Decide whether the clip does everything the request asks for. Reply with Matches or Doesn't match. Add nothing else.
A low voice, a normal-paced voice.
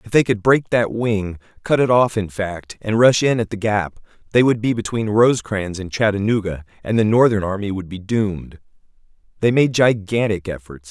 Matches